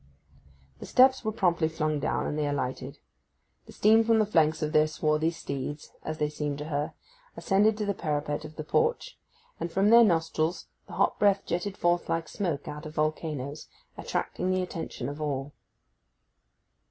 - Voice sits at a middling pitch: Yes, medium, 160 Hz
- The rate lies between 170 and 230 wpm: Yes, average, 175 wpm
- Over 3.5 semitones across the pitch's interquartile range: Yes, average, 4.4 semitones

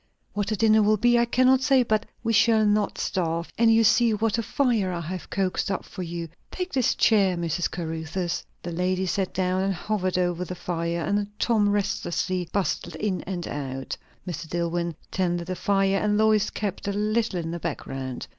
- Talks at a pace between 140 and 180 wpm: No, average, 195 wpm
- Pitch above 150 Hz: Yes, high, 190 Hz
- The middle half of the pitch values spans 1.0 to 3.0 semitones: No, average, 3.8 semitones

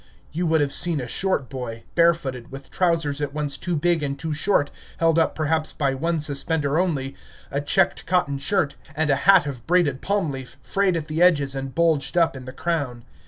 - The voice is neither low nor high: Yes, medium, 150 Hz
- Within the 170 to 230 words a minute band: Yes, fast, 205 wpm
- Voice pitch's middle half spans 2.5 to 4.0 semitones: Yes, average, 3.5 semitones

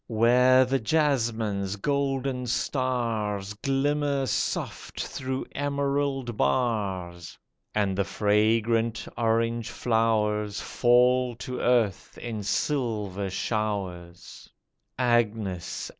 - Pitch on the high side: No, low, 115 Hz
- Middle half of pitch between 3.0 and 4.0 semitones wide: Yes, average, 3.6 semitones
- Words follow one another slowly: Yes, slow, 85 wpm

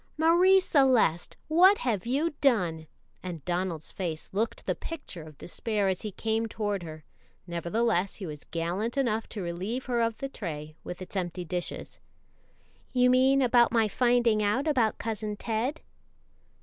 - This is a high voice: Yes, high, 215 Hz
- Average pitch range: No, wide, 5.9 semitones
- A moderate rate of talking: Yes, average, 155 wpm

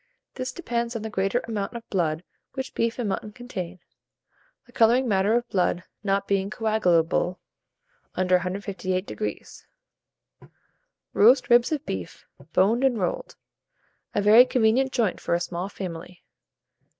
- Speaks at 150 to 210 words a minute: No, slow, 135 wpm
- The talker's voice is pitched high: Yes, high, 205 Hz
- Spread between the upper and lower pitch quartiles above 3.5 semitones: Yes, average, 4.5 semitones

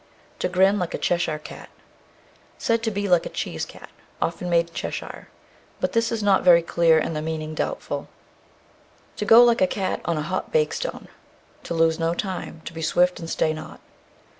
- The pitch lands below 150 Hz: No, medium, 175 Hz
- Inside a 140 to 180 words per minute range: No, average, 195 wpm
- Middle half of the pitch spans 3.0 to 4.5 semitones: Yes, average, 3.7 semitones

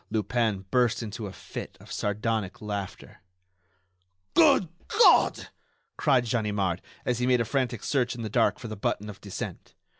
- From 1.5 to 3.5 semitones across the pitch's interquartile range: Yes, average, 3.1 semitones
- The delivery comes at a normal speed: Yes, average, 155 wpm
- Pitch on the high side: No, low, 110 Hz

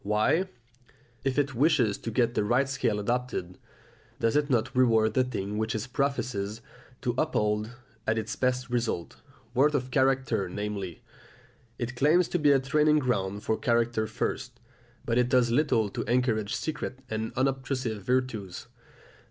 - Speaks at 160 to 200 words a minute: No, average, 150 wpm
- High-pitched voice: No, low, 120 Hz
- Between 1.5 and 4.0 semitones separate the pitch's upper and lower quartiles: Yes, average, 3.5 semitones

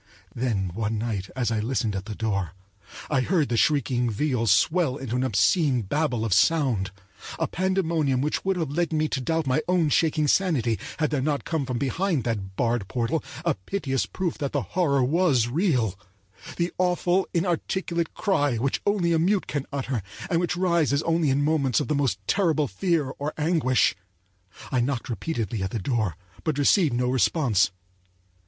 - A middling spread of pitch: No, wide, 5.9 semitones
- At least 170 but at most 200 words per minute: Yes, average, 175 wpm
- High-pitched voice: No, medium, 140 Hz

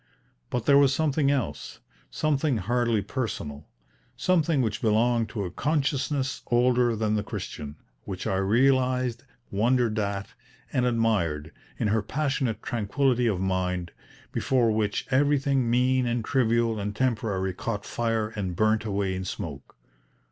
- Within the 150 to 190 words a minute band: No, slow, 135 wpm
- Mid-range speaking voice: No, low, 115 Hz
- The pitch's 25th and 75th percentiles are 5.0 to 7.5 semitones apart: No, average, 4.2 semitones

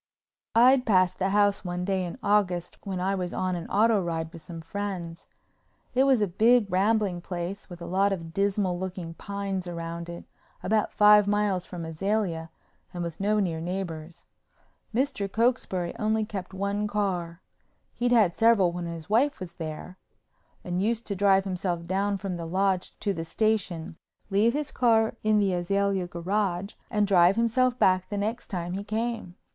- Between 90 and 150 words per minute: No, average, 170 wpm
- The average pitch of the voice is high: Yes, high, 195 Hz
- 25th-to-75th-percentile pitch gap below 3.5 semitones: Yes, average, 3.1 semitones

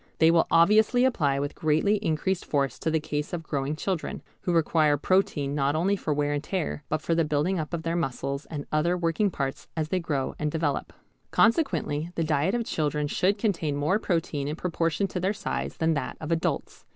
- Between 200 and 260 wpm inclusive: Yes, fast, 205 wpm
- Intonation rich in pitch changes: No, average, 3.5 semitones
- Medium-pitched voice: Yes, medium, 160 Hz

